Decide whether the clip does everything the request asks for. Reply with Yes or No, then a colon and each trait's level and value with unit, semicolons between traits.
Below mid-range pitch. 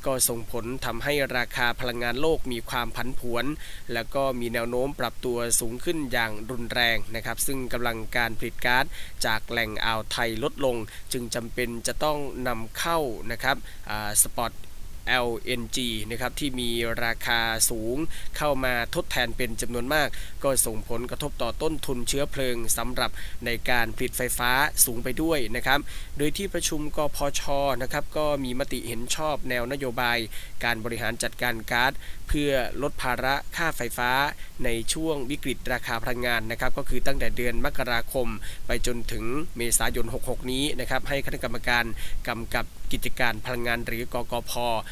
Yes: low, 120 Hz